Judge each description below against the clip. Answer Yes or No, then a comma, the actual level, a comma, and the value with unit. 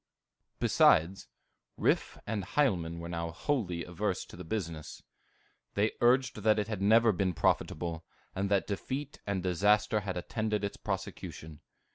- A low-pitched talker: Yes, low, 100 Hz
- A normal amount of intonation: Yes, average, 3.9 semitones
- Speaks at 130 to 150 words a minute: Yes, average, 140 wpm